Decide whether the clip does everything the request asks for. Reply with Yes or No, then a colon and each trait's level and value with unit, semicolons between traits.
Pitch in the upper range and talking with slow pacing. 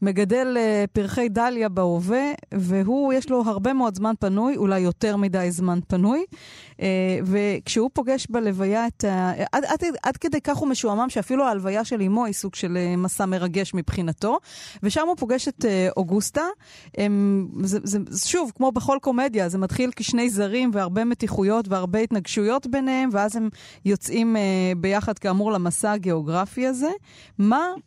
No: high, 215 Hz; average, 145 wpm